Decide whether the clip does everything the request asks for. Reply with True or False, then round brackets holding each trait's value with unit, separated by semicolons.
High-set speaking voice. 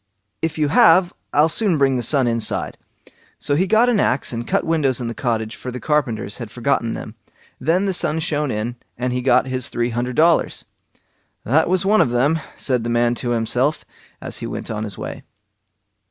False (130 Hz)